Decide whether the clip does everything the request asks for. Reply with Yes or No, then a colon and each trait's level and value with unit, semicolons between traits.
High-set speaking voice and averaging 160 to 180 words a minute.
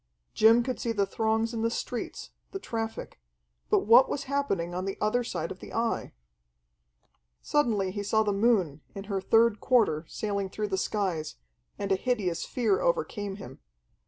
Yes: high, 215 Hz; average, 170 wpm